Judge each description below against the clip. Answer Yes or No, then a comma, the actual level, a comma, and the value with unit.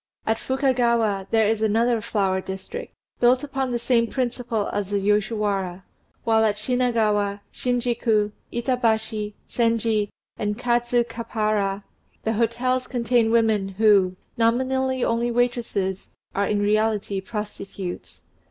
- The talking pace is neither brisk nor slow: No, slow, 115 wpm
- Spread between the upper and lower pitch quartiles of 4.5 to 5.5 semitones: No, narrow, 2.6 semitones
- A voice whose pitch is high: Yes, high, 225 Hz